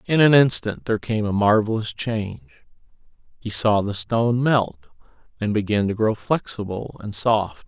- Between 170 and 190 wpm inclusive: No, average, 155 wpm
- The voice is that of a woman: No, male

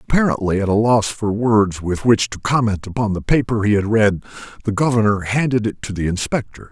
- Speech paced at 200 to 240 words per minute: Yes, fast, 205 wpm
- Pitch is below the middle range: Yes, low, 110 Hz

